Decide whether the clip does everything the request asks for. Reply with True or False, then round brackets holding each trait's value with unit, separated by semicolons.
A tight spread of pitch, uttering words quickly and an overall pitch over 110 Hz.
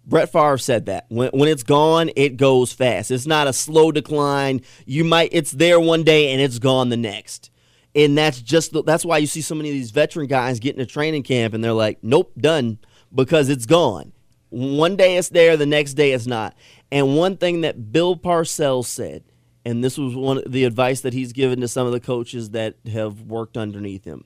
False (4.1 semitones; 220 wpm; 135 Hz)